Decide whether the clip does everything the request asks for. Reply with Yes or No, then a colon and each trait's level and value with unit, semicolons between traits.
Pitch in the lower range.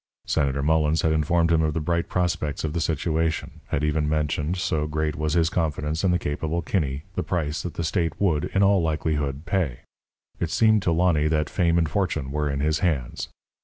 Yes: very low, 80 Hz